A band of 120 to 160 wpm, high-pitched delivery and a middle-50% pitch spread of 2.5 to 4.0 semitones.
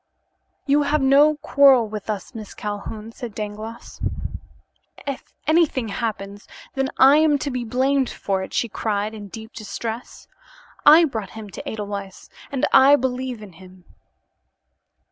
No: average, 145 wpm; high, 230 Hz; average, 4.7 semitones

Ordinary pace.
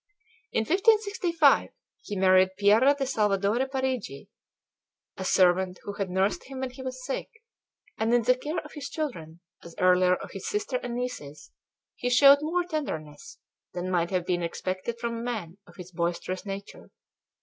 Yes: average, 165 wpm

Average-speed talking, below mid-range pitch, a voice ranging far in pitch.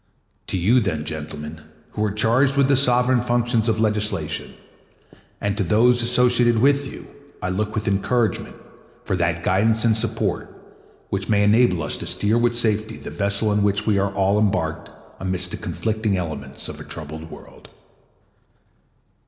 No: average, 160 wpm; low, 105 Hz; average, 3.8 semitones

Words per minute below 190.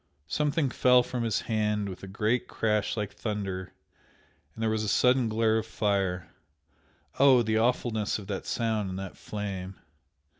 Yes: average, 160 wpm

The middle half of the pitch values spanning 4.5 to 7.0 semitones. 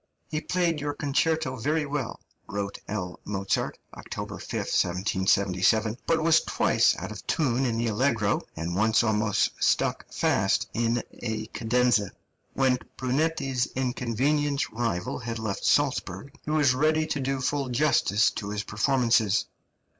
Yes: average, 5.2 semitones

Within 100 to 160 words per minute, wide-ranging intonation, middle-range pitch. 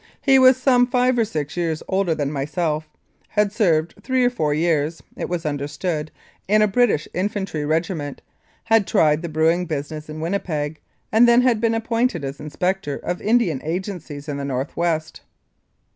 No: average, 170 wpm; wide, 5.9 semitones; medium, 170 Hz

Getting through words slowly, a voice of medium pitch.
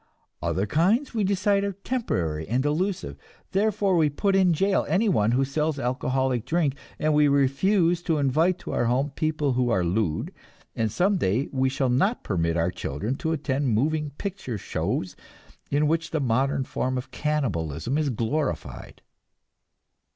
No: average, 160 wpm; medium, 145 Hz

